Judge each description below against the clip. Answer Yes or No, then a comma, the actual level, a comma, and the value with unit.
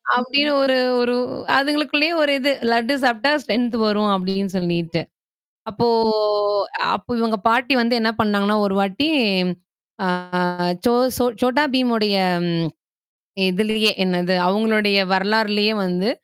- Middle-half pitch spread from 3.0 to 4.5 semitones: Yes, average, 4.0 semitones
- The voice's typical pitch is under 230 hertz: Yes, high, 220 Hz